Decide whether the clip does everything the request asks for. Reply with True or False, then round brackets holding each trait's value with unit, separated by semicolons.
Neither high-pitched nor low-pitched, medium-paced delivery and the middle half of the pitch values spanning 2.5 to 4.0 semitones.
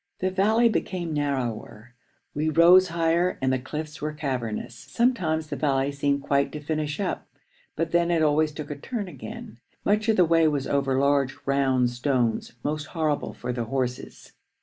True (150 Hz; 170 wpm; 3.7 semitones)